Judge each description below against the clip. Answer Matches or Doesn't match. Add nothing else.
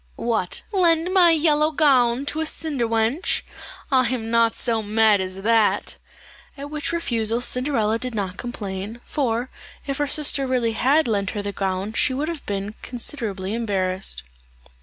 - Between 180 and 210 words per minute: Doesn't match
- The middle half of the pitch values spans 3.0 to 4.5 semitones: Doesn't match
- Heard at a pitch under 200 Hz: Doesn't match